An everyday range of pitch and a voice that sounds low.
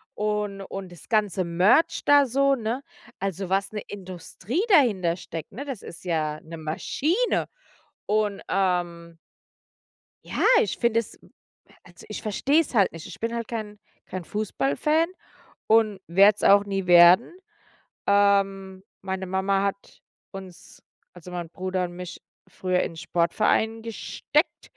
No: average, 3.6 semitones; high, 195 Hz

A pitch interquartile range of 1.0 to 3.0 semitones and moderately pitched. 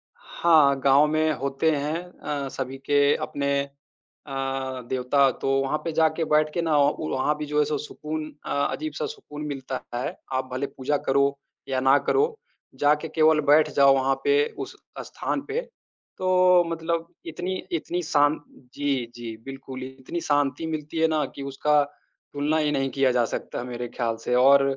Yes: average, 2.7 semitones; medium, 145 Hz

